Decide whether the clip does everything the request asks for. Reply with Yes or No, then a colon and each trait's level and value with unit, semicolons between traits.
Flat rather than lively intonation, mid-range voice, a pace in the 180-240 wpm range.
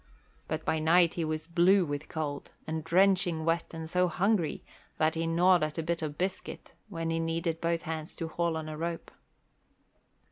Yes: narrow, 1.6 semitones; medium, 165 Hz; average, 190 wpm